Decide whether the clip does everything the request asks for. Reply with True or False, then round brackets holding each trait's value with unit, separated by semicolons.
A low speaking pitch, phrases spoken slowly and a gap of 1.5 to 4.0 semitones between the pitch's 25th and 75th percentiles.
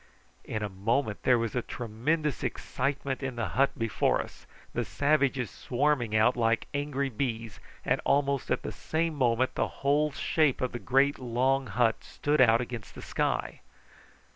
False (130 Hz; 165 wpm; 3.3 semitones)